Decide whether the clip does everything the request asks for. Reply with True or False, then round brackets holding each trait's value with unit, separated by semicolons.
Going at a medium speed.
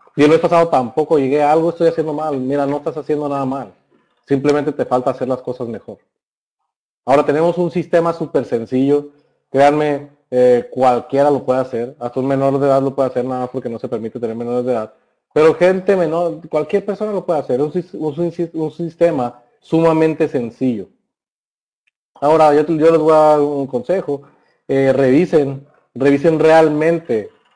True (180 wpm)